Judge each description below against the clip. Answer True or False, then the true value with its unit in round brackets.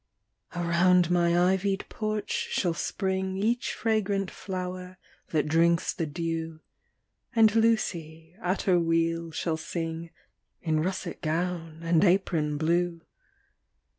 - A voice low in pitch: False (175 Hz)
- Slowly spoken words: True (110 wpm)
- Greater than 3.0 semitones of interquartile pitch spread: False (2.4 semitones)